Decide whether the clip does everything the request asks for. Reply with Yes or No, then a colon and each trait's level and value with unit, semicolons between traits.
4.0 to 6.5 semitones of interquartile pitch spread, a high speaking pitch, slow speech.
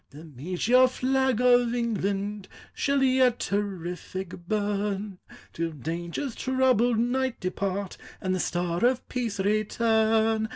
Yes: average, 4.7 semitones; high, 210 Hz; slow, 115 wpm